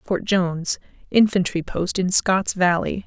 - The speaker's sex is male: No, female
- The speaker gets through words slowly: Yes, slow, 115 wpm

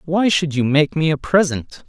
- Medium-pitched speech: Yes, medium, 155 Hz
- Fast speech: Yes, fast, 225 wpm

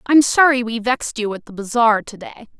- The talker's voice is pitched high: Yes, high, 235 Hz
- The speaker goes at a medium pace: No, fast, 230 wpm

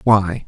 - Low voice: Yes, low, 100 Hz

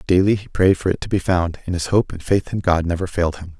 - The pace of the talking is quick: Yes, fast, 300 wpm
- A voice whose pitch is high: No, very low, 90 Hz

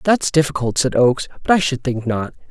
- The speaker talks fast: Yes, fast, 215 wpm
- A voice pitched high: No, medium, 140 Hz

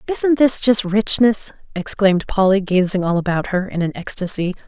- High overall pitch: Yes, high, 200 Hz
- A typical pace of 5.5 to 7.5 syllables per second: No, 5.1 syllables/s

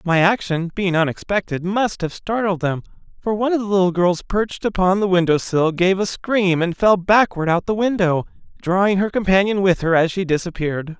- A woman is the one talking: No, male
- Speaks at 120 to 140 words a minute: No, average, 195 wpm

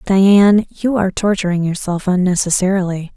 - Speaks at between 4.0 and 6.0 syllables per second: Yes, 5.3 syllables/s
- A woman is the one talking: Yes, female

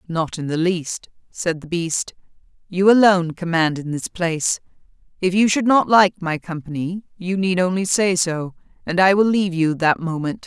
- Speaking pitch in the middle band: Yes, medium, 175 Hz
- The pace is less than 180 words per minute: No, average, 185 wpm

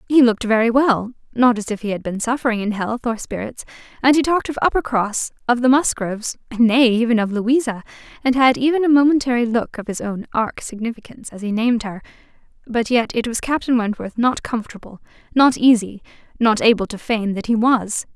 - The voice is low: No, high, 235 Hz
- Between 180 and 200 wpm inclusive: Yes, average, 195 wpm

